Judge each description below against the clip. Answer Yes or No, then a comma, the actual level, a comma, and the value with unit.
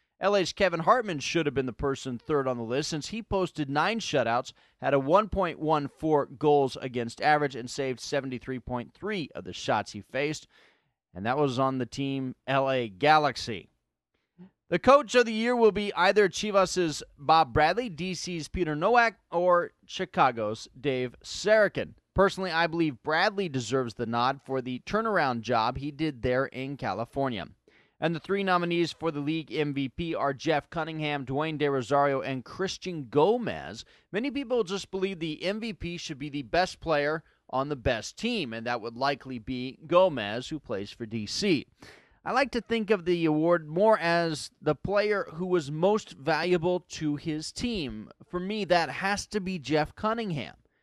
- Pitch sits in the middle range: Yes, medium, 155 Hz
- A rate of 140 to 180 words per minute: Yes, average, 165 wpm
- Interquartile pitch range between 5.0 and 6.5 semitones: Yes, wide, 5.5 semitones